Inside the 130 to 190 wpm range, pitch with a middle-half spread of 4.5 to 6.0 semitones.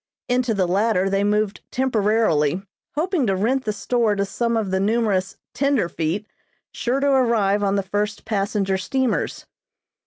No: average, 150 wpm; average, 3.4 semitones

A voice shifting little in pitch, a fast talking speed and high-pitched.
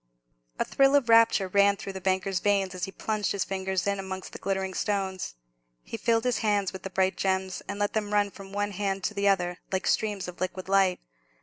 Yes: narrow, 1.5 semitones; fast, 220 wpm; high, 195 Hz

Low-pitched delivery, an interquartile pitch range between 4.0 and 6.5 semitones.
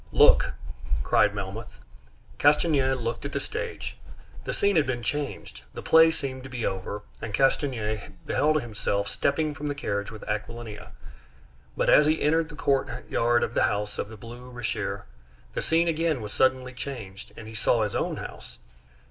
Yes: low, 125 Hz; average, 5.2 semitones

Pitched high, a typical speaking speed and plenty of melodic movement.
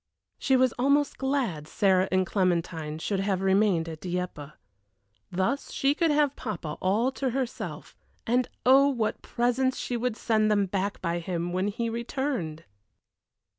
Yes: high, 210 Hz; average, 150 wpm; wide, 6.1 semitones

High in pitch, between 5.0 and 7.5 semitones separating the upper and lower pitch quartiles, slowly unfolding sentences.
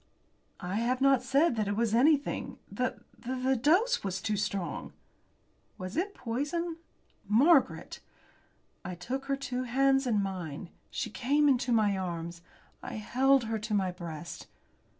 No: high, 235 Hz; wide, 5.6 semitones; average, 145 wpm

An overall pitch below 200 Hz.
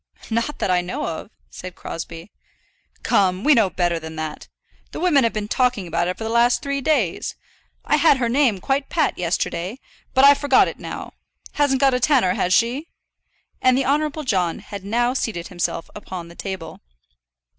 No: high, 225 Hz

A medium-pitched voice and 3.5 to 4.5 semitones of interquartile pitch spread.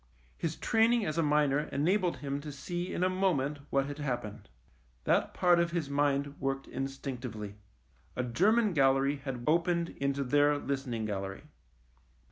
Yes: medium, 145 Hz; average, 3.9 semitones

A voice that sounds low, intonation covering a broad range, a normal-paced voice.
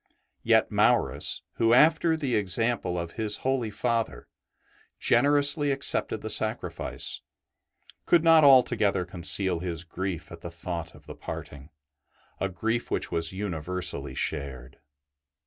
No: low, 100 Hz; wide, 6.8 semitones; slow, 125 wpm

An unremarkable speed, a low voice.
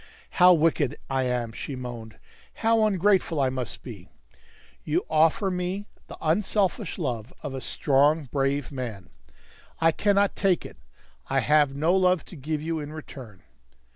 No: average, 150 wpm; medium, 150 Hz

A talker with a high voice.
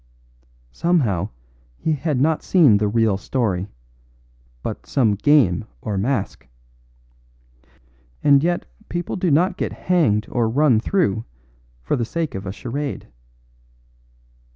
No: low, 130 Hz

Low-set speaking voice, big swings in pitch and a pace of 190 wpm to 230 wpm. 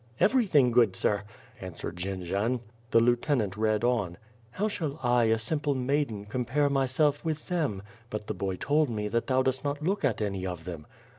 Yes: low, 120 Hz; wide, 5.7 semitones; average, 200 wpm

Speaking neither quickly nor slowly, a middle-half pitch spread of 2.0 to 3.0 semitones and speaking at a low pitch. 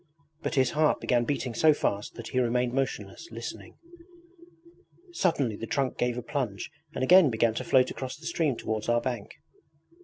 No: average, 175 wpm; average, 3.5 semitones; low, 125 Hz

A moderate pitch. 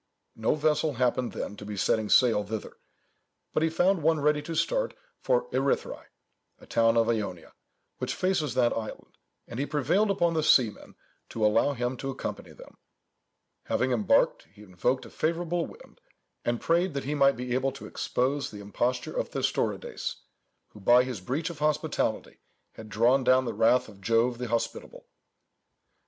No: low, 130 Hz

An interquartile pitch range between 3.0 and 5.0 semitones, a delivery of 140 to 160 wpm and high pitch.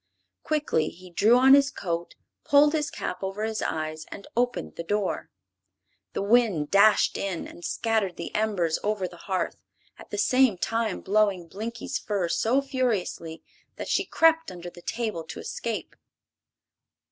No: wide, 5.4 semitones; average, 155 wpm; high, 205 Hz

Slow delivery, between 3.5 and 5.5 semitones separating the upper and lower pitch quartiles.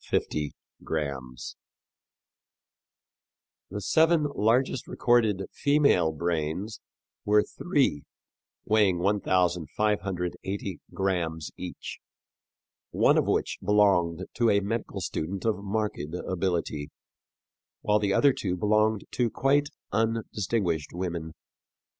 Yes: slow, 85 wpm; average, 4.1 semitones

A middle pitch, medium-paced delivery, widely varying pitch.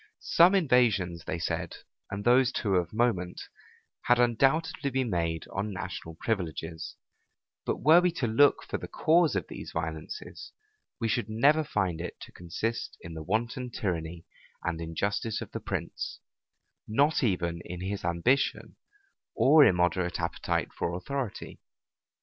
No: low, 100 Hz; average, 145 wpm; wide, 6.5 semitones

